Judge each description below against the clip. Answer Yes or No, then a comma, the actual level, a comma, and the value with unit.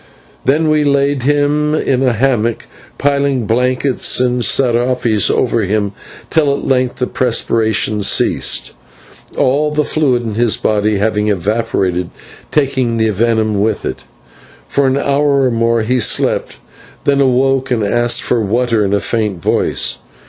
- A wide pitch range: No, average, 3.9 semitones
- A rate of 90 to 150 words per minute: Yes, average, 145 wpm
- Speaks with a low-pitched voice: Yes, low, 125 Hz